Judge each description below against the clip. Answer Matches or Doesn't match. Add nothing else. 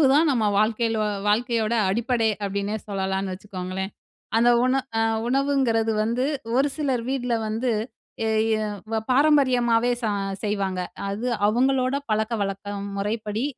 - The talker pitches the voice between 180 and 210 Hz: Doesn't match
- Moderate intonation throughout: Matches